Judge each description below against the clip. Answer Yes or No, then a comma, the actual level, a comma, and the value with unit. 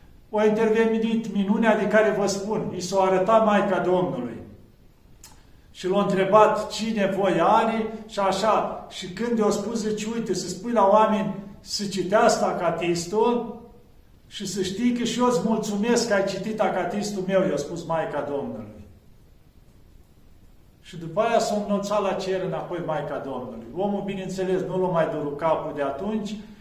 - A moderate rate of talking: Yes, average, 155 wpm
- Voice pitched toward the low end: No, high, 200 Hz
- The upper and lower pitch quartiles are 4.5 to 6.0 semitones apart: No, average, 3.0 semitones